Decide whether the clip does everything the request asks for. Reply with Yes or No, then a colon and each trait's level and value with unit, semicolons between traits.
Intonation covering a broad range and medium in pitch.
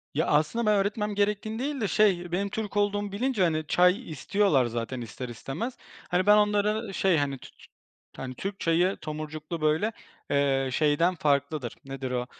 Yes: wide, 6.4 semitones; medium, 175 Hz